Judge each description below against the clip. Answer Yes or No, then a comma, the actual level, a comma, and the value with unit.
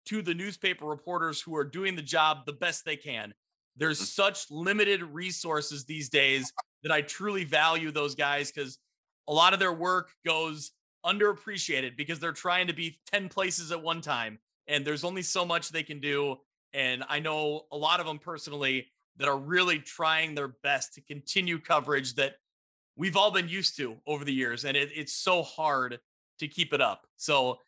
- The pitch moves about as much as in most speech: Yes, average, 3.7 semitones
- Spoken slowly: No, average, 190 wpm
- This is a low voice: No, medium, 155 Hz